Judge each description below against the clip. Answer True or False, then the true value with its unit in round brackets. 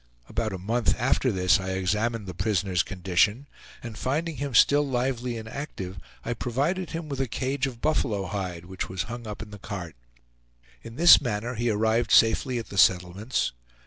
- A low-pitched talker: True (115 Hz)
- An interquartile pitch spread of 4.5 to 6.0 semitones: True (5.0 semitones)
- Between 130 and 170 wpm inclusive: False (180 wpm)